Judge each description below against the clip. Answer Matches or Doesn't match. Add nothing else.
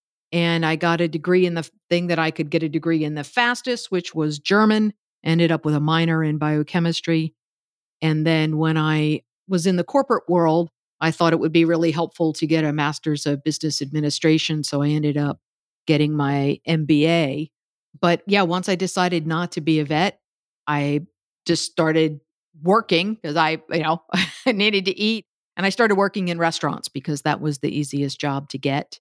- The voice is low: Doesn't match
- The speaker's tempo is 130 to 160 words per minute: Doesn't match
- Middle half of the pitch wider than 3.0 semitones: Doesn't match